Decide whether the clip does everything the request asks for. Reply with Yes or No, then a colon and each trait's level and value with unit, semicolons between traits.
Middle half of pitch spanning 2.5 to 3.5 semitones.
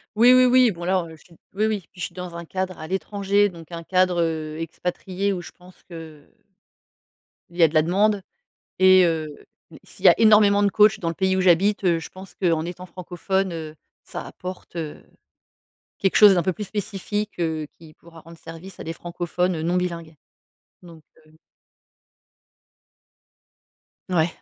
Yes: average, 2.8 semitones